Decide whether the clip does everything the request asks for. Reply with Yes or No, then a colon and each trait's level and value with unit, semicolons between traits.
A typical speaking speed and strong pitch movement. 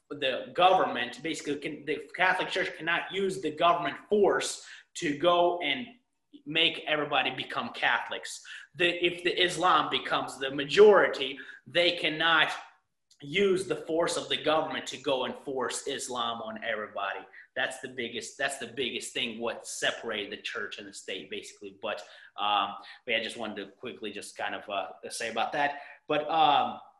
Yes: average, 160 wpm; wide, 7.7 semitones